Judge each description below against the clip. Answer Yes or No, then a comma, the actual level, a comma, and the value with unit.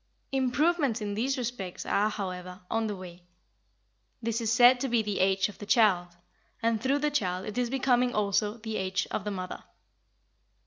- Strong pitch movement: No, average, 4.3 semitones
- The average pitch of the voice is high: Yes, high, 215 Hz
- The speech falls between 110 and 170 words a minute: No, average, 180 wpm